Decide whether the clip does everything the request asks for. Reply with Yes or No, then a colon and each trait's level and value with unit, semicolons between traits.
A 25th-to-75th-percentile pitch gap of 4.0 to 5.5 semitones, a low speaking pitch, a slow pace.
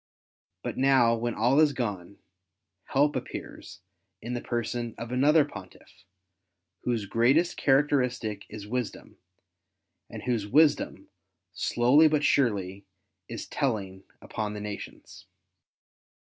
Yes: average, 4.4 semitones; low, 120 Hz; slow, 110 wpm